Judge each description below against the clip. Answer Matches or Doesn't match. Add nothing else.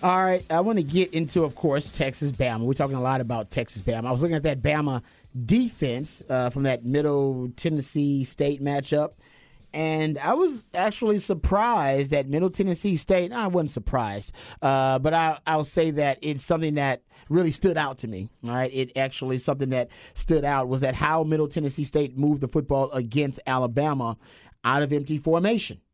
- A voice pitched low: Doesn't match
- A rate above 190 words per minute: Doesn't match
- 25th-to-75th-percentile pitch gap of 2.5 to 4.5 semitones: Matches